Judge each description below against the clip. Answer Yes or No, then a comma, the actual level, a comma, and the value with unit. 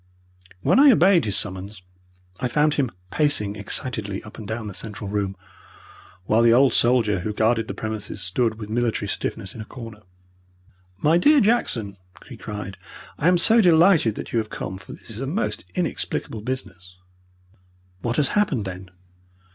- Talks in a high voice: No, low, 115 Hz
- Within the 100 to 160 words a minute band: No, average, 170 wpm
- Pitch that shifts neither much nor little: No, wide, 6.1 semitones